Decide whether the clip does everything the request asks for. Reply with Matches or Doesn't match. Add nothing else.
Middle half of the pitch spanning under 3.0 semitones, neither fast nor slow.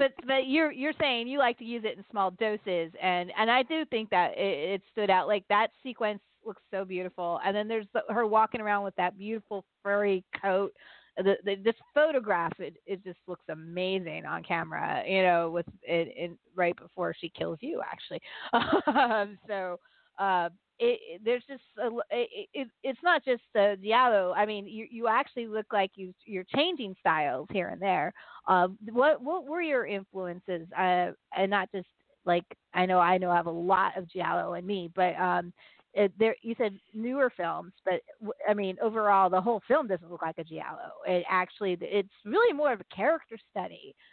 Doesn't match